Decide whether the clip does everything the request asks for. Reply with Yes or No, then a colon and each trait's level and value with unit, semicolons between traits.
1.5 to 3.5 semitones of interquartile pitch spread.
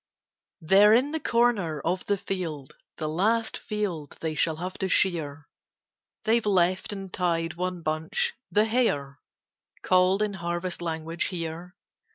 No: average, 4.2 semitones